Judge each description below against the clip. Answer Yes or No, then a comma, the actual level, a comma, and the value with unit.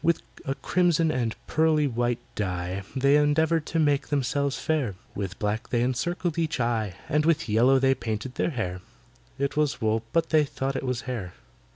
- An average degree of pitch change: Yes, average, 4.9 semitones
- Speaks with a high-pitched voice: No, low, 135 Hz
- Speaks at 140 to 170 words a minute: No, average, 180 wpm